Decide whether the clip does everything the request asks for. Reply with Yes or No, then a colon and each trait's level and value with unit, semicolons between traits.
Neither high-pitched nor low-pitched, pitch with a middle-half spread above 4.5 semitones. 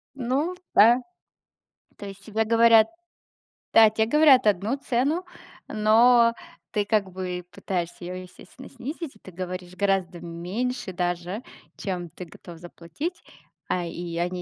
No: high, 205 Hz; average, 4.9 semitones